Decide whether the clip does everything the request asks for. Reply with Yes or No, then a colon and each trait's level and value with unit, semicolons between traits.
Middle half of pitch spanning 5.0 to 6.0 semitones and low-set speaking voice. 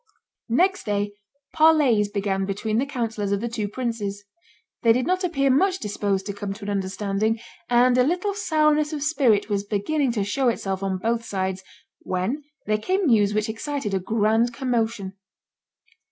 No: average, 5.3 semitones; high, 225 Hz